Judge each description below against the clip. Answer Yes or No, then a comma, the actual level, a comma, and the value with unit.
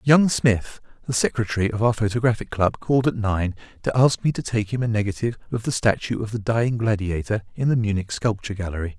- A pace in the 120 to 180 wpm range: No, fast, 205 wpm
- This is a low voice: Yes, low, 110 Hz